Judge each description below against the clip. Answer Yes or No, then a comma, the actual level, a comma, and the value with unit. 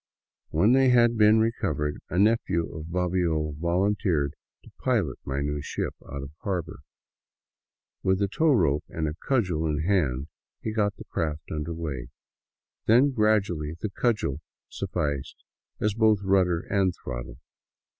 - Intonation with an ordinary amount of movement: No, wide, 5.9 semitones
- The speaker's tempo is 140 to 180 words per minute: Yes, average, 145 wpm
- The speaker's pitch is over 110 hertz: No, very low, 90 Hz